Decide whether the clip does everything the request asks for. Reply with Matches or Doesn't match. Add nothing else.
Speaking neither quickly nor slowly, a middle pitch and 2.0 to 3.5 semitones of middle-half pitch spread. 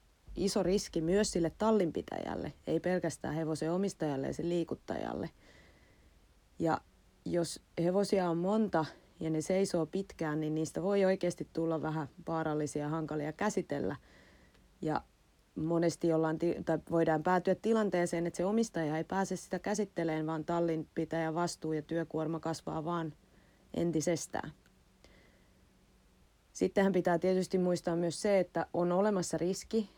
Matches